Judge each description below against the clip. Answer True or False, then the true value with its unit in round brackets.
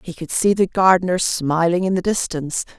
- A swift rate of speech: False (195 wpm)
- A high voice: False (180 Hz)